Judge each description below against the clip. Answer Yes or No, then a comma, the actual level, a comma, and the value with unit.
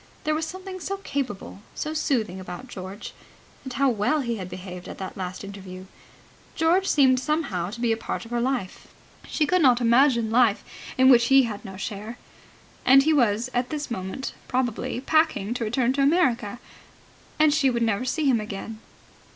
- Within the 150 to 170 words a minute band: No, average, 185 wpm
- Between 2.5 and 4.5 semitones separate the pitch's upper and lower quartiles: No, average, 5.2 semitones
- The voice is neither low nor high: No, high, 245 Hz